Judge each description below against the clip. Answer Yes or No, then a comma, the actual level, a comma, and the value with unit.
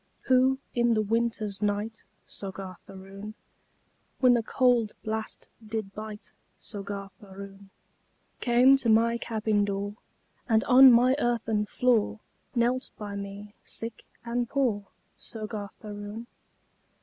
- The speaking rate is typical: No, slow, 115 wpm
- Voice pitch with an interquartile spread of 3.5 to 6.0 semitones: No, average, 2.7 semitones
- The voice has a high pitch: Yes, high, 220 Hz